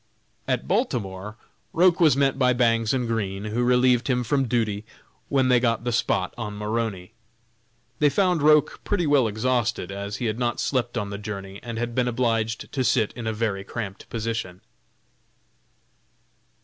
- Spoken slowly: No, average, 165 wpm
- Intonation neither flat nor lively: Yes, average, 3.2 semitones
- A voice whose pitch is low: Yes, low, 115 Hz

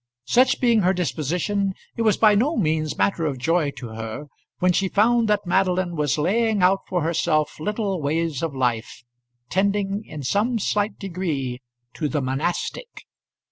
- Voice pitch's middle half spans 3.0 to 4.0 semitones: No, average, 5.2 semitones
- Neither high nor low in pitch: Yes, medium, 180 Hz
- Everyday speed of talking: Yes, average, 160 wpm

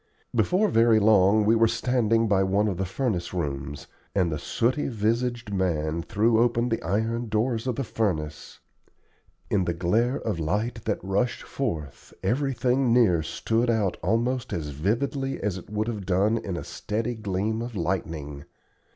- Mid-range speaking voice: No, low, 110 Hz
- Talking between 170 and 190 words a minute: No, average, 160 wpm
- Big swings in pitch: No, average, 4.3 semitones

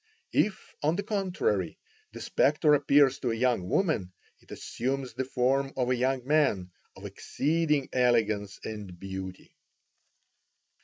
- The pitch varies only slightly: No, average, 5.3 semitones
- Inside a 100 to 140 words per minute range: Yes, slow, 135 wpm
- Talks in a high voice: No, low, 130 Hz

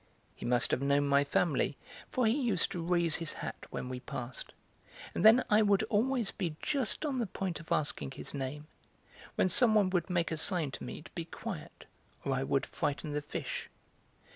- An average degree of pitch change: No, wide, 6.6 semitones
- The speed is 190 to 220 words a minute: Yes, average, 200 wpm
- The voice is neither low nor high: Yes, medium, 170 Hz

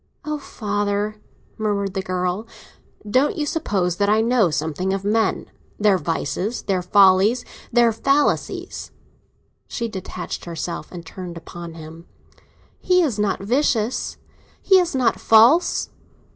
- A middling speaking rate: No, slow, 125 wpm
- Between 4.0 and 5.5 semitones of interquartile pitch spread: Yes, average, 4.7 semitones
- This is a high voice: Yes, high, 205 Hz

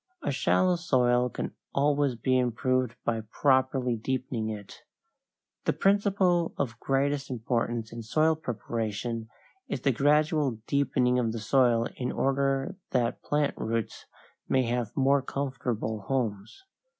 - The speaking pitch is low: Yes, low, 130 Hz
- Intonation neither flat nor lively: Yes, average, 3.3 semitones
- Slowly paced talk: Yes, slow, 125 wpm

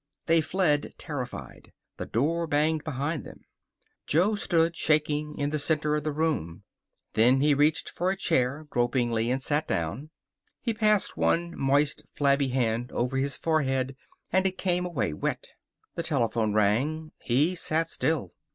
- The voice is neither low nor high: Yes, medium, 150 Hz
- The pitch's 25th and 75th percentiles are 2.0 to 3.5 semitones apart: No, average, 4.0 semitones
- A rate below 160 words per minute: Yes, average, 150 wpm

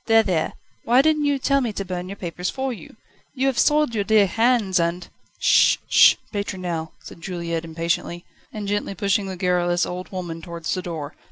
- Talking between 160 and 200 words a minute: Yes, average, 195 wpm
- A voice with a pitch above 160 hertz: Yes, medium, 185 Hz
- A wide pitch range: No, average, 4.5 semitones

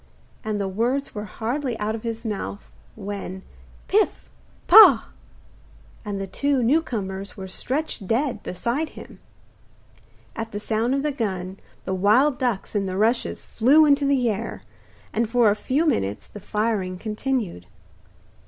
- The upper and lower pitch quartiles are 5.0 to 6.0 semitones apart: No, average, 4.5 semitones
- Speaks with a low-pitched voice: No, high, 220 Hz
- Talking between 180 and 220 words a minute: No, average, 150 wpm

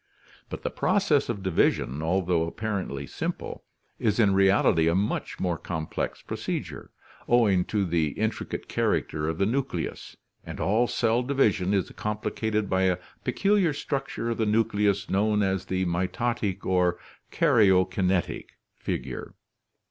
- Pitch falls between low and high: No, low, 100 Hz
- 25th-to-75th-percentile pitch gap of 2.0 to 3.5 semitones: No, average, 3.9 semitones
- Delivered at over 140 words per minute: No, slow, 135 wpm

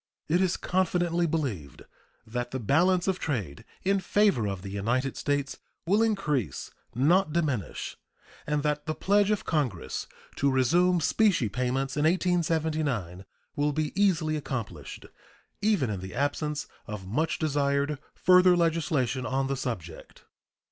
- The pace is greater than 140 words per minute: No, slow, 135 wpm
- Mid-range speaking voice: Yes, medium, 150 Hz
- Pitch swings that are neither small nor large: No, wide, 5.7 semitones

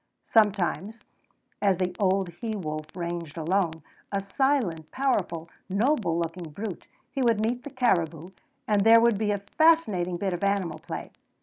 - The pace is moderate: Yes, average, 150 wpm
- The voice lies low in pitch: No, high, 195 Hz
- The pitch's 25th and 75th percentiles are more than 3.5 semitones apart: Yes, average, 4.6 semitones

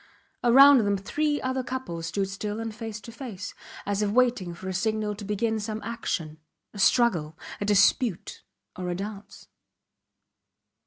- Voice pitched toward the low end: No, high, 210 Hz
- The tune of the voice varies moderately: Yes, average, 3.4 semitones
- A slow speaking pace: No, average, 155 wpm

